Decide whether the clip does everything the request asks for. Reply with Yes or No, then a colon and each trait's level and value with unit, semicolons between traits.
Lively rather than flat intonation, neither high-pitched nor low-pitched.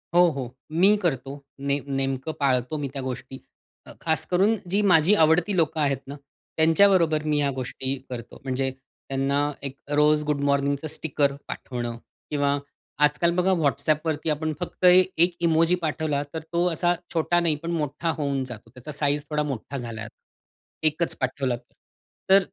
No: average, 3.3 semitones; medium, 150 Hz